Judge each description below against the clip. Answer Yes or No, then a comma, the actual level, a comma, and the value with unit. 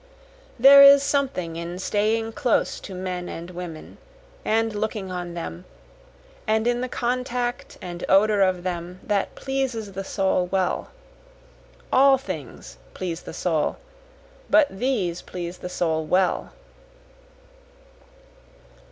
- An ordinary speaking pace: No, slow, 120 wpm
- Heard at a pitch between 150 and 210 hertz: Yes, high, 190 Hz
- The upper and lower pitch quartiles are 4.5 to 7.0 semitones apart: Yes, average, 5.3 semitones